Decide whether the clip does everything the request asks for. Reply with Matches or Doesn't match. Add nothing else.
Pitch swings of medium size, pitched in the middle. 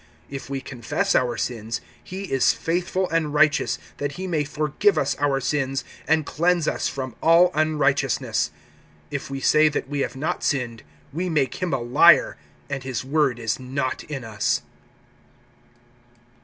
Matches